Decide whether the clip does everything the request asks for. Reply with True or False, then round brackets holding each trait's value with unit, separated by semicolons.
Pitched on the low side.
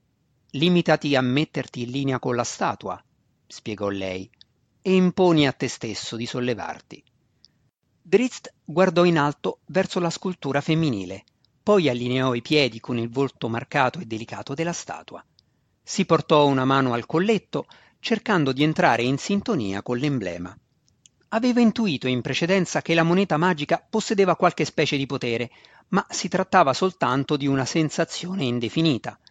False (145 Hz)